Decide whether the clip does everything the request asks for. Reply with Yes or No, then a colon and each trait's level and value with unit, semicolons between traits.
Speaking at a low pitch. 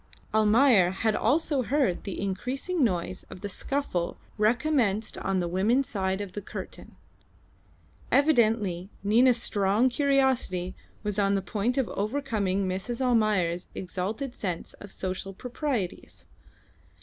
No: high, 210 Hz